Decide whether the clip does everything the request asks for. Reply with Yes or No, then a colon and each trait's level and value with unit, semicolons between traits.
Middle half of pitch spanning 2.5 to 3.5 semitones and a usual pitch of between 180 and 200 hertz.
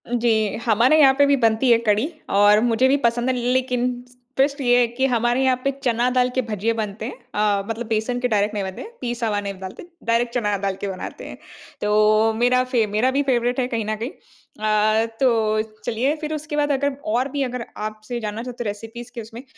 No: average, 2.9 semitones; high, 235 Hz